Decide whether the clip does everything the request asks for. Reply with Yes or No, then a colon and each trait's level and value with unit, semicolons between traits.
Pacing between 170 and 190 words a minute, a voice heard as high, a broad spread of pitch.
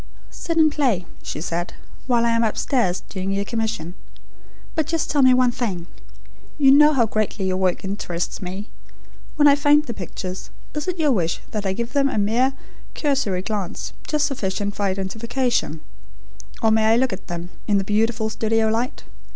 Yes: average, 180 wpm; high, 220 Hz; wide, 5.7 semitones